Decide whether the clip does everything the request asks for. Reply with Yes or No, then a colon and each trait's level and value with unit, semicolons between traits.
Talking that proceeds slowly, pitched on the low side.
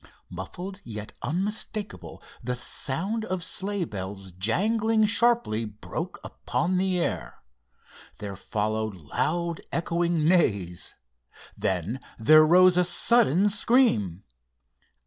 No: slow, 100 wpm; medium, 170 Hz